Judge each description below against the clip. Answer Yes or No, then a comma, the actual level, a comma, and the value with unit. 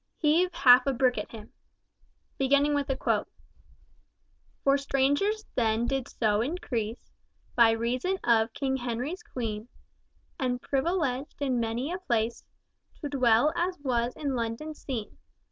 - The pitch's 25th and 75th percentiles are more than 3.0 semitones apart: Yes, average, 3.6 semitones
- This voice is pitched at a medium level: No, very high, 260 Hz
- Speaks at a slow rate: Yes, slow, 120 wpm